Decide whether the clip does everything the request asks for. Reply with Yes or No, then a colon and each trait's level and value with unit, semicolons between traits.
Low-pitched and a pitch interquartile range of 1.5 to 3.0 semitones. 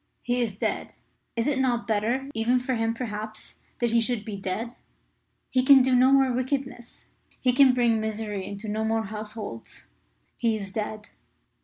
No: high, 230 Hz; average, 2.7 semitones